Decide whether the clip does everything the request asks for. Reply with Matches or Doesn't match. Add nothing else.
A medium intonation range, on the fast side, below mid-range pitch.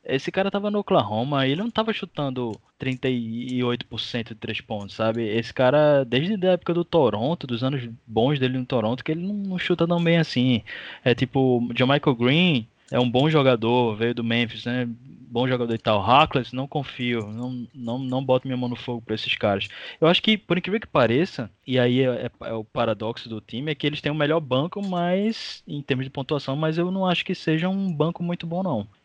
Doesn't match